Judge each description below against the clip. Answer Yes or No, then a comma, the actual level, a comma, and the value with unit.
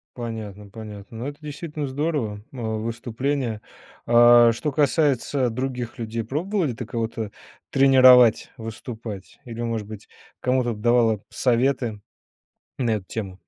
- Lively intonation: No, average, 3.0 semitones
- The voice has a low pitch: Yes, low, 120 Hz